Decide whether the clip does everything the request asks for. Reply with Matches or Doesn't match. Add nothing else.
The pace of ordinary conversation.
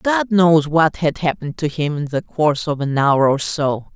Doesn't match